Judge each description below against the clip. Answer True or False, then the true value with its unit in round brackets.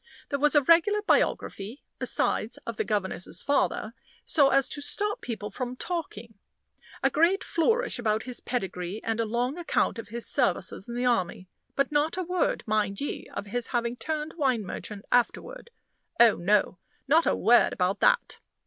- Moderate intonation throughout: False (6.0 semitones)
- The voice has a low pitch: False (245 Hz)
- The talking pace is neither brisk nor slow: True (170 wpm)